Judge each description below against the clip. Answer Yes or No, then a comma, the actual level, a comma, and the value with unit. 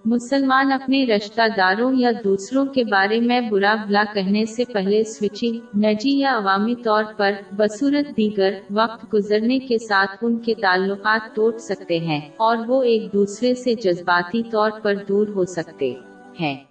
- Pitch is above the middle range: Yes, high, 215 Hz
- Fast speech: No, average, 160 wpm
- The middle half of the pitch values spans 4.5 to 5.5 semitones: No, average, 3.0 semitones